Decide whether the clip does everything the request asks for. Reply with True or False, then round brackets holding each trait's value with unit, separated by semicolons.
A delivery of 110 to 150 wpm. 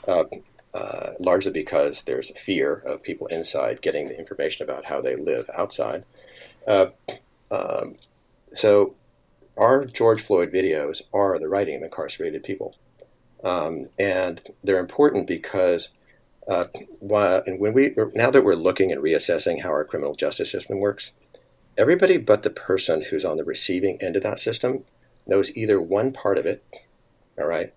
False (160 wpm)